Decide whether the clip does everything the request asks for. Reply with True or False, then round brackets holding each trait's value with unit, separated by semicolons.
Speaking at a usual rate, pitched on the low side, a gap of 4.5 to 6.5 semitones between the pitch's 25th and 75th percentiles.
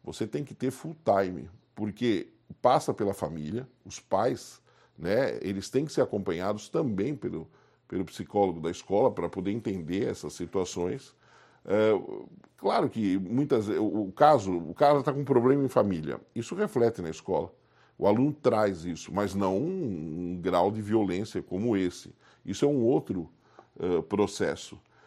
True (155 wpm; 100 Hz; 5.5 semitones)